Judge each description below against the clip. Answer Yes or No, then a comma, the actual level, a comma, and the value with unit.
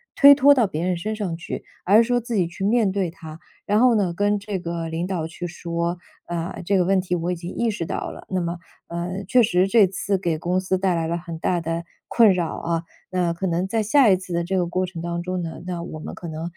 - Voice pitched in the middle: Yes, medium, 180 Hz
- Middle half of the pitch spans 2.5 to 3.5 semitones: Yes, average, 2.8 semitones